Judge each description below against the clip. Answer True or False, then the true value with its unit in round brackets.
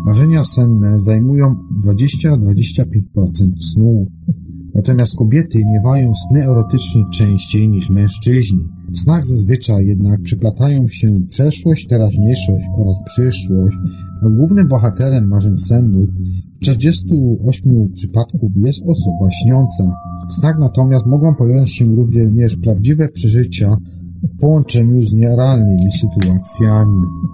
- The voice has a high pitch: False (110 Hz)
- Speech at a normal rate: False (100 wpm)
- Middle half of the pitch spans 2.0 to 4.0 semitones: False (4.9 semitones)